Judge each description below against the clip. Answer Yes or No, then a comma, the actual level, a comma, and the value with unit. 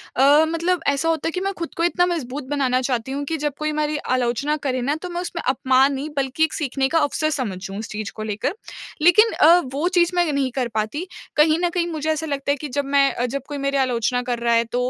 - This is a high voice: Yes, very high, 285 Hz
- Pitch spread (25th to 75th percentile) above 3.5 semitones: Yes, average, 3.9 semitones